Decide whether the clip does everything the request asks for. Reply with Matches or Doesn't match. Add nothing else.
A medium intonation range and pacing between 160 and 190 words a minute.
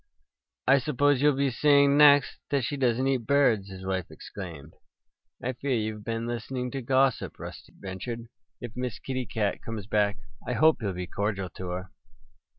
Matches